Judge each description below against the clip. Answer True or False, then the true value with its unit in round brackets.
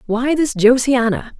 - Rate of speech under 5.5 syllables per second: True (4.1 syllables/s)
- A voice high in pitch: True (245 Hz)